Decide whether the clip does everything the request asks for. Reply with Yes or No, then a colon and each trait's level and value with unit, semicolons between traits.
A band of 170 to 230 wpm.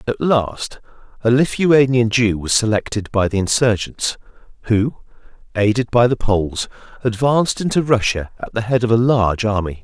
No: average, 150 wpm